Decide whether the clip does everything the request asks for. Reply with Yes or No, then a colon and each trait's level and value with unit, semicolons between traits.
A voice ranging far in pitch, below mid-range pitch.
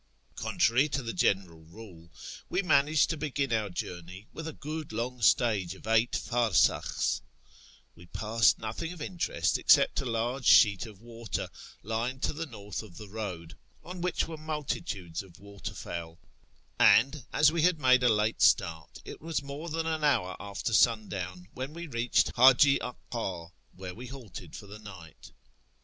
Yes: wide, 6.6 semitones; low, 115 Hz